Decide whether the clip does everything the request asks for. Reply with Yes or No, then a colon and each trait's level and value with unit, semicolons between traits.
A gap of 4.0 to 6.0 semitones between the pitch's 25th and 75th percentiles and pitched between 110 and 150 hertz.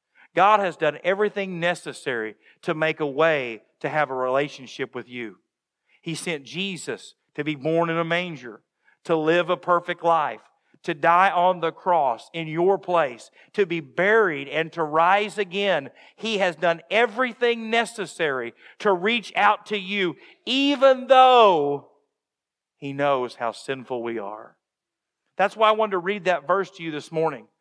No: average, 4.6 semitones; medium, 170 Hz